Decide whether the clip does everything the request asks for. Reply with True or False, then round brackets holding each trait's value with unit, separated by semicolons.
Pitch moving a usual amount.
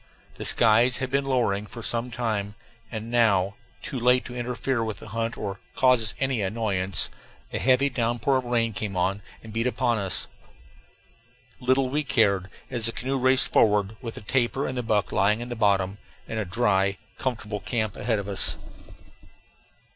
True (3.4 semitones)